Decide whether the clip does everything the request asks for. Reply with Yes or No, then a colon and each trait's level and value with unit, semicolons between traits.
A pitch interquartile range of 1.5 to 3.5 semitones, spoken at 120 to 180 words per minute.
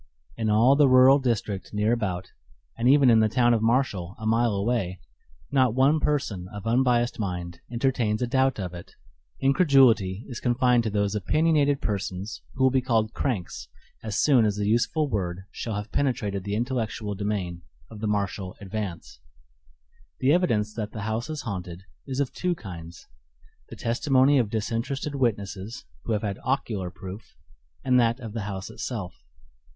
No: average, 4.2 semitones; average, 165 wpm